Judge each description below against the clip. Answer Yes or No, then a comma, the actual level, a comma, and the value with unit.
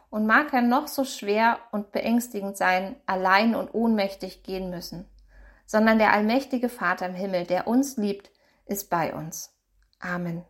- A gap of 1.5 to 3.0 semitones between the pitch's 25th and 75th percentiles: No, average, 4.1 semitones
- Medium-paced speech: Yes, average, 155 wpm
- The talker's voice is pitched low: No, high, 205 Hz